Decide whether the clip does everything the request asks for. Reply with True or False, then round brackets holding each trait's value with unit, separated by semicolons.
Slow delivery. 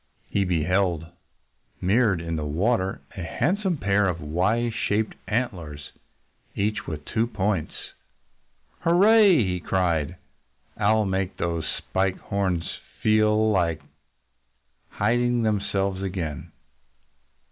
True (105 wpm)